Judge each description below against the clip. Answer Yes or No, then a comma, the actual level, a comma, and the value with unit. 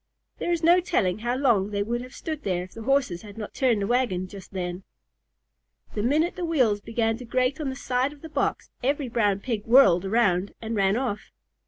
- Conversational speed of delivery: No, fast, 215 wpm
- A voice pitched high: Yes, high, 230 Hz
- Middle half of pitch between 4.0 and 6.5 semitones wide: Yes, average, 4.9 semitones